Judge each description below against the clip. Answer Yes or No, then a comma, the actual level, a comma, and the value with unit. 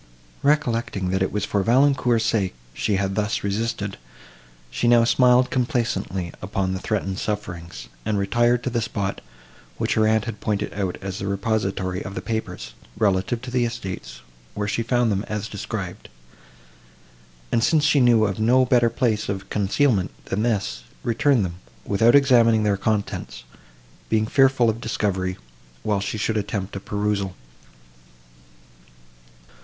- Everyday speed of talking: Yes, average, 150 wpm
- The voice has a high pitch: No, low, 105 Hz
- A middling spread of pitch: Yes, average, 3.4 semitones